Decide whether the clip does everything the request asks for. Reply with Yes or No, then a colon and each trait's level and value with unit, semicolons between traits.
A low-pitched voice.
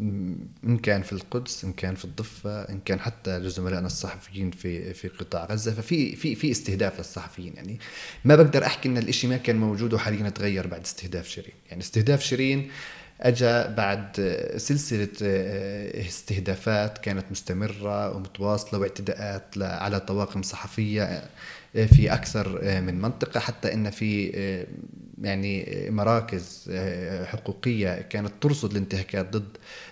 Yes: low, 100 Hz